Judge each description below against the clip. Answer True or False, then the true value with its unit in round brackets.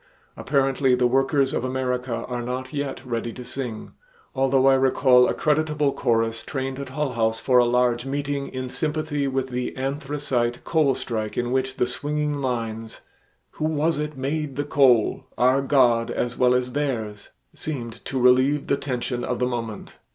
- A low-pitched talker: True (130 Hz)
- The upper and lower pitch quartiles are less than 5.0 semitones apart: True (2.5 semitones)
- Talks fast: False (170 wpm)